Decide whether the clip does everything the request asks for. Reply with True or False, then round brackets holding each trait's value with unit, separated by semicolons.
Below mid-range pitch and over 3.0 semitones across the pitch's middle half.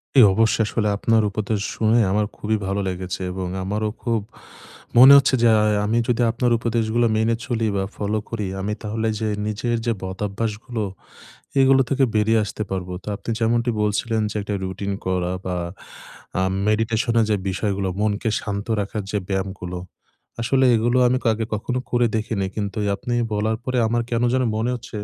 False (110 Hz; 2.5 semitones)